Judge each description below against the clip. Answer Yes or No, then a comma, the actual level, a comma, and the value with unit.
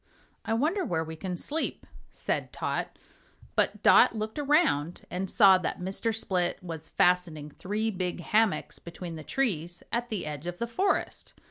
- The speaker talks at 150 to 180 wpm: Yes, average, 160 wpm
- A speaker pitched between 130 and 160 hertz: No, medium, 185 Hz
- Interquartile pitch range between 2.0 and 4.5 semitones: No, average, 4.9 semitones